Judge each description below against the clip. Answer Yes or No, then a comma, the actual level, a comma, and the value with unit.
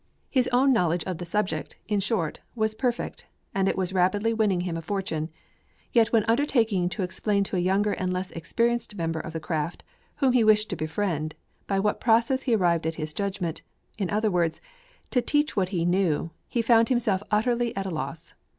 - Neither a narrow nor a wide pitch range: Yes, average, 4.7 semitones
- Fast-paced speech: No, average, 195 wpm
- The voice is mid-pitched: No, high, 195 Hz